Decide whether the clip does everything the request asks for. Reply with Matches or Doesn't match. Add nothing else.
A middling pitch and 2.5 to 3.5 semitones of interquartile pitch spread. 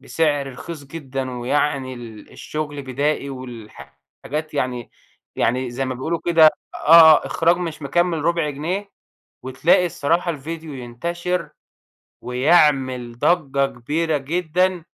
Doesn't match